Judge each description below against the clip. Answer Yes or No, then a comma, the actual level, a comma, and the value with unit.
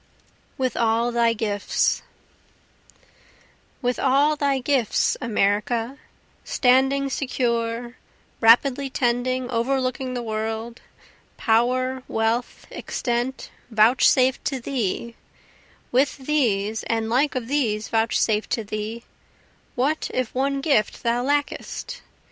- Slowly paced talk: Yes, slow, 100 wpm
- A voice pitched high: Yes, high, 245 Hz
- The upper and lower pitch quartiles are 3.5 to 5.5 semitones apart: No, average, 2.7 semitones